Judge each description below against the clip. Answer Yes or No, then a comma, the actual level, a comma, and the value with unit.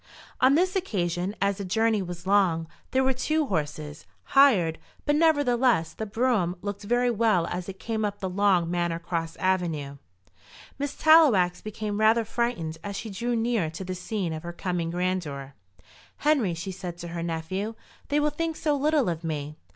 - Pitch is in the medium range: No, high, 195 Hz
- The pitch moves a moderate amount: No, wide, 5.8 semitones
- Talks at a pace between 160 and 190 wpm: Yes, average, 175 wpm